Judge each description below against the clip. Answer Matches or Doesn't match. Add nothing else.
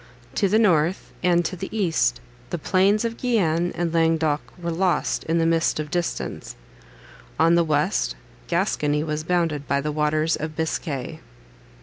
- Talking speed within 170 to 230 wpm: Doesn't match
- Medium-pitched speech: Matches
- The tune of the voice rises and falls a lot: Doesn't match